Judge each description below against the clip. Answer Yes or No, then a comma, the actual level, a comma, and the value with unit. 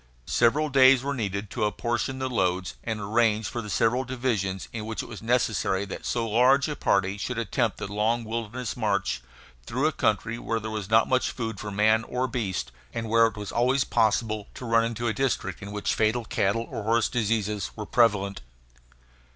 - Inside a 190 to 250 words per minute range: Yes, average, 195 wpm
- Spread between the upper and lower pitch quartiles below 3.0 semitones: Yes, narrow, 2.6 semitones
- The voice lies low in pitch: Yes, low, 115 Hz